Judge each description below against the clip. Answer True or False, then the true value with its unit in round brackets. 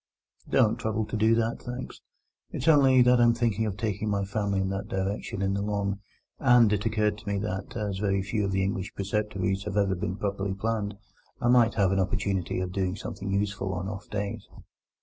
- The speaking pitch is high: False (100 Hz)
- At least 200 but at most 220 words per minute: True (205 wpm)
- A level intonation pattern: True (2.2 semitones)